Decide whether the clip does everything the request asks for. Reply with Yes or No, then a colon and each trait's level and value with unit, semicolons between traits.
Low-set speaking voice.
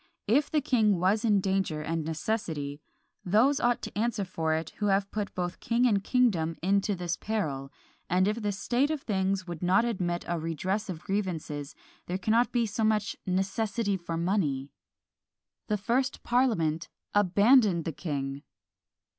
No: high, 195 Hz